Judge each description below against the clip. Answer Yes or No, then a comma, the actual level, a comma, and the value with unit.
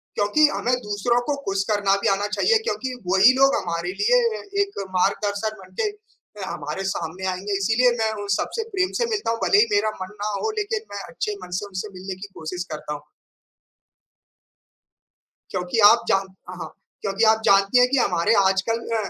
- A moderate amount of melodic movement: No, wide, 5.7 semitones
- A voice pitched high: Yes, high, 205 Hz